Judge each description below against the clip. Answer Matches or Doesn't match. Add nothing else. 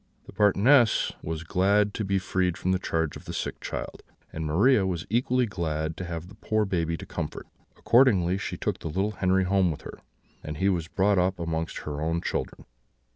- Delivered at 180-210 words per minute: Matches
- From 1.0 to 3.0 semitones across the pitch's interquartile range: Doesn't match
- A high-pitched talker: Doesn't match